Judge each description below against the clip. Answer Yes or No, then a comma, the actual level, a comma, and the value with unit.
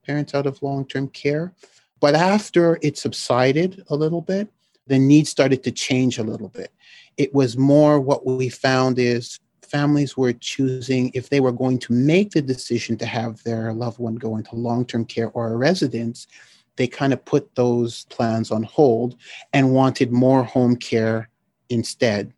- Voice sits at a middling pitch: No, low, 130 Hz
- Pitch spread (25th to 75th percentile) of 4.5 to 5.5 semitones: No, average, 3.3 semitones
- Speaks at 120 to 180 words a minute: Yes, average, 170 wpm